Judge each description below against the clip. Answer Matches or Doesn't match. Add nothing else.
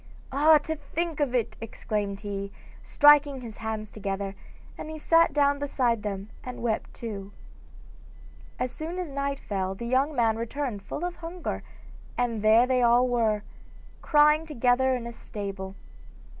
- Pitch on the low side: Doesn't match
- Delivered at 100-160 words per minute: Matches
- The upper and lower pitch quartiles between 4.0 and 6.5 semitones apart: Matches